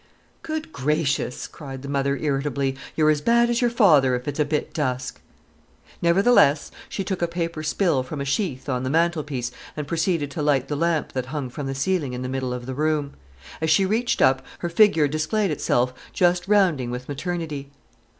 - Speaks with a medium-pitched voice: Yes, medium, 150 Hz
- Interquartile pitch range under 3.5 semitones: No, average, 4.2 semitones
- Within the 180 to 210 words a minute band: Yes, average, 190 wpm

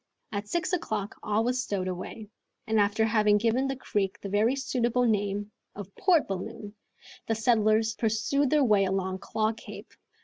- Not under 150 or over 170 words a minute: Yes, average, 165 wpm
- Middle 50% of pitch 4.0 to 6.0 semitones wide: No, average, 3.1 semitones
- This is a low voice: No, high, 215 Hz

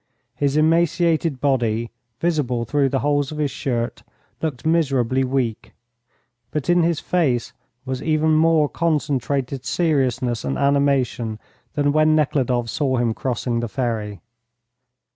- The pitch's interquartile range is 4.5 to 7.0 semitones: No, average, 4.0 semitones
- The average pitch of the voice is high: No, medium, 140 Hz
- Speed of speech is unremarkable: No, slow, 125 wpm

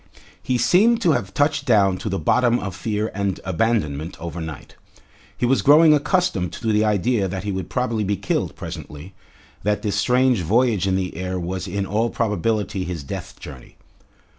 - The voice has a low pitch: Yes, low, 105 Hz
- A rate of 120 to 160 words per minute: No, average, 175 wpm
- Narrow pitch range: No, average, 4.7 semitones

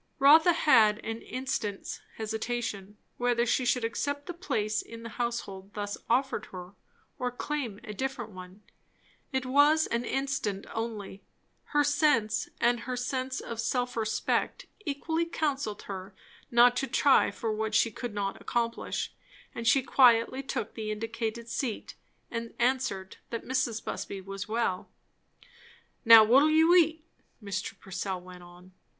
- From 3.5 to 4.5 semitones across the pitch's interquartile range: Yes, average, 4.0 semitones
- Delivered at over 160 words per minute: No, average, 145 wpm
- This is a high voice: Yes, high, 230 Hz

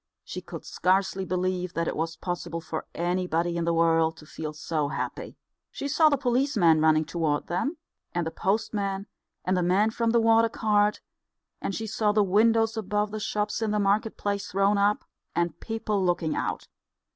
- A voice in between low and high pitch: No, high, 195 Hz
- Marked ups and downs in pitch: No, average, 4.2 semitones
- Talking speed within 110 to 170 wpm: No, average, 180 wpm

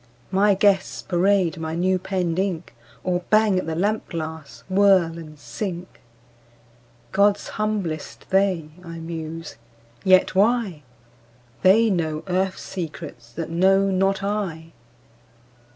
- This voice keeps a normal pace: No, slow, 120 wpm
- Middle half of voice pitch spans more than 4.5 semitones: No, average, 3.1 semitones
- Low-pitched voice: No, medium, 185 Hz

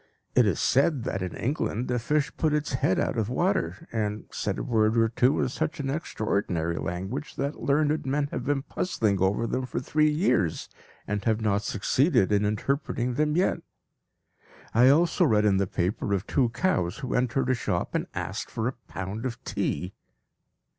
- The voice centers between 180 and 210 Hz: No, low, 120 Hz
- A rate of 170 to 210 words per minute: Yes, average, 185 wpm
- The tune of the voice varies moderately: No, wide, 5.7 semitones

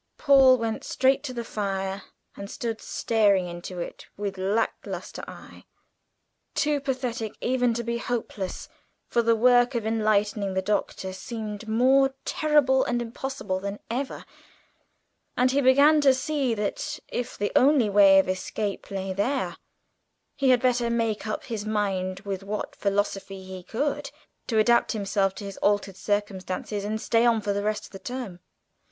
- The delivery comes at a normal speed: Yes, average, 160 wpm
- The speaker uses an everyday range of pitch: Yes, average, 4.0 semitones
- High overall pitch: Yes, high, 220 Hz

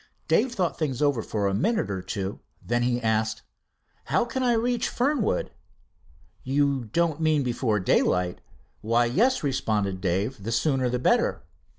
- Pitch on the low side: Yes, low, 125 Hz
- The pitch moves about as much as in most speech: No, wide, 7.0 semitones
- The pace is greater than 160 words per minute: No, average, 155 wpm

